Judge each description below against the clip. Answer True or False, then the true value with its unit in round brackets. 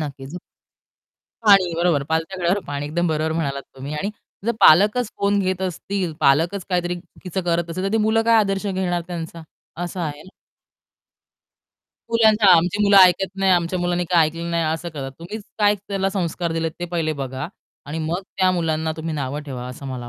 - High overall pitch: False (175 Hz)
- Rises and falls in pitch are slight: False (3.3 semitones)